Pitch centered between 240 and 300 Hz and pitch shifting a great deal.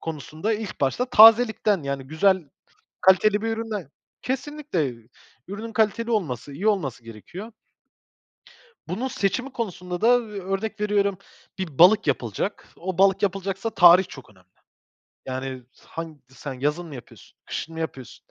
No: high, 190 Hz; wide, 6.7 semitones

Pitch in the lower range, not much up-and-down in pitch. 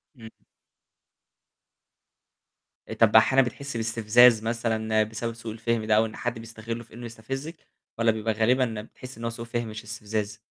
Yes: low, 115 Hz; narrow, 1.2 semitones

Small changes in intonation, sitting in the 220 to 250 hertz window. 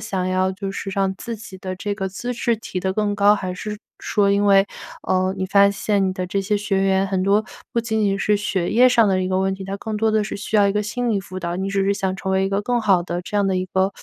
No: narrow, 1.7 semitones; high, 195 Hz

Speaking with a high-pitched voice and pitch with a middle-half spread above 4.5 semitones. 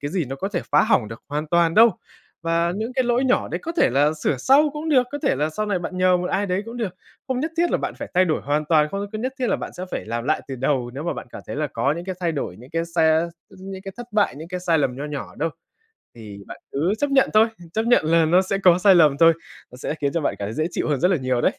No: medium, 170 Hz; wide, 5.5 semitones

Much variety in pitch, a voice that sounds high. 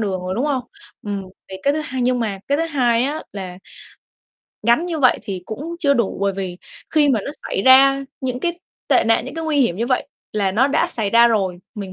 Yes: wide, 5.9 semitones; high, 240 Hz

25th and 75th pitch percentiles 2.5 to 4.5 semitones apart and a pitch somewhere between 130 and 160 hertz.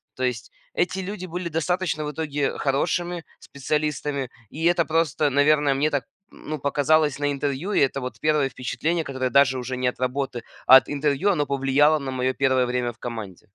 Yes: average, 3.1 semitones; medium, 140 Hz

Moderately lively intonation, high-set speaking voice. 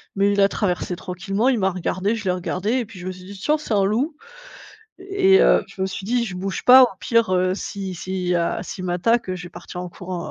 Yes: average, 3.9 semitones; high, 195 Hz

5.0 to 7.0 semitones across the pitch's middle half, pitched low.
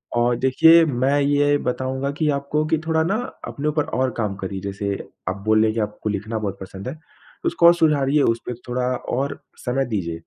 Yes: average, 5.3 semitones; low, 130 Hz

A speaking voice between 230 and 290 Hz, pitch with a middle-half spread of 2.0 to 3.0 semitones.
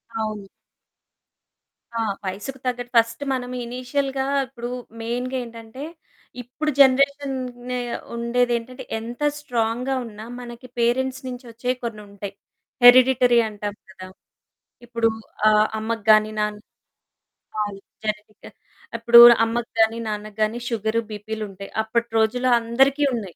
Yes: high, 235 Hz; average, 2.7 semitones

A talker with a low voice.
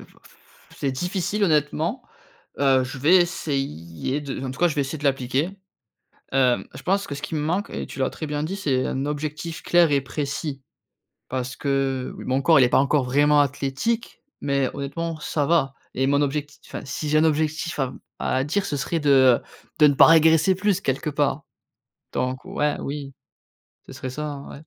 No: medium, 145 Hz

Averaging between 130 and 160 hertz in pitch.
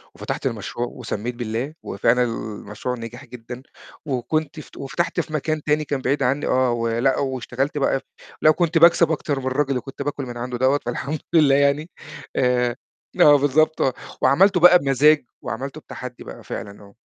Yes: low, 135 Hz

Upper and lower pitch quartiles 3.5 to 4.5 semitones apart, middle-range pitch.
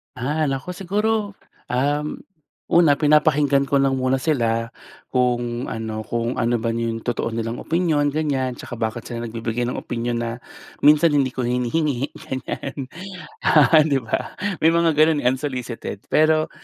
No: average, 4.2 semitones; low, 130 Hz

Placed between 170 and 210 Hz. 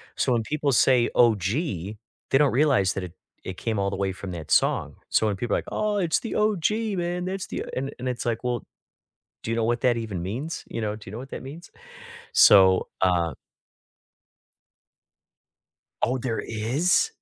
No: low, 120 Hz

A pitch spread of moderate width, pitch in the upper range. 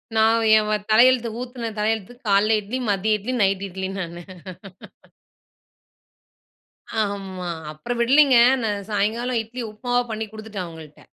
Yes: average, 3.4 semitones; high, 215 Hz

